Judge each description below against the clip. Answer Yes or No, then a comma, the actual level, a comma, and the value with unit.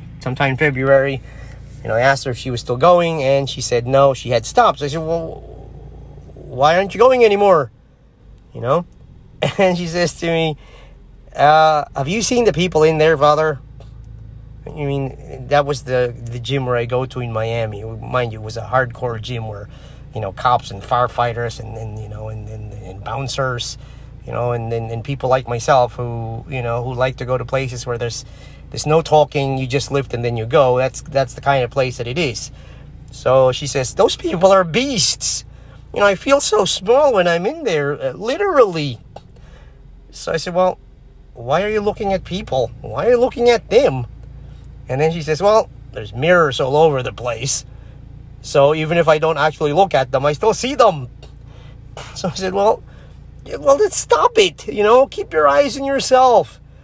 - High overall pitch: No, low, 135 Hz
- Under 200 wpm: No, fast, 205 wpm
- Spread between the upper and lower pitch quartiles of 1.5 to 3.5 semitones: No, average, 4.9 semitones